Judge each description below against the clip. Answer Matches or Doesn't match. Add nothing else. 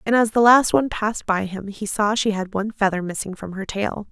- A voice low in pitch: Doesn't match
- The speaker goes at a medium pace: Doesn't match